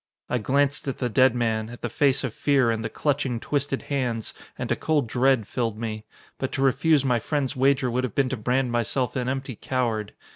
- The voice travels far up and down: No, average, 2.7 semitones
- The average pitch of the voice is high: No, low, 130 Hz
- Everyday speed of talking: No, fast, 215 wpm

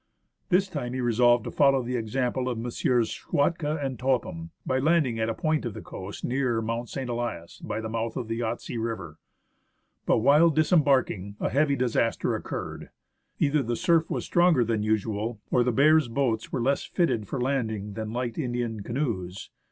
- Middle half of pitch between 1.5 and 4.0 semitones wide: Yes, average, 3.6 semitones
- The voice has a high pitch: No, low, 120 Hz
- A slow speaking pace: No, average, 180 wpm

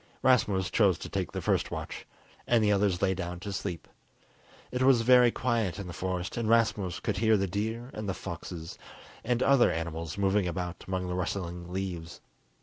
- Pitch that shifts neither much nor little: Yes, average, 4.0 semitones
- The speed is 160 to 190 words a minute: Yes, average, 180 wpm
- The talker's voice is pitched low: Yes, very low, 95 Hz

